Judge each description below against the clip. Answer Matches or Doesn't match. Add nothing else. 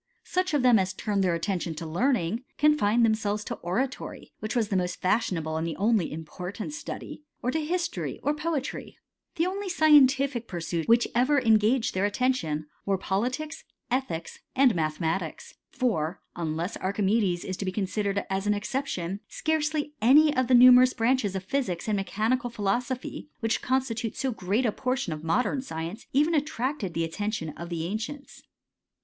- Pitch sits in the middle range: Doesn't match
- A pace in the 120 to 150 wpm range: Doesn't match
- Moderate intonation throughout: Doesn't match